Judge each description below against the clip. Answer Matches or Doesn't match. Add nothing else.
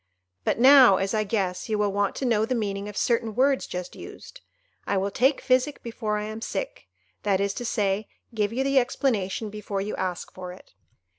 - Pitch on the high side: Matches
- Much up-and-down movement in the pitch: Doesn't match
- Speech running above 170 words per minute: Matches